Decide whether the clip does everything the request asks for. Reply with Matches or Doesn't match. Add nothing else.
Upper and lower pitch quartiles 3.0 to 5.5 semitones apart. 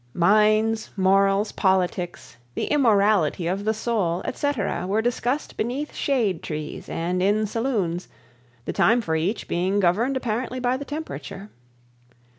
Matches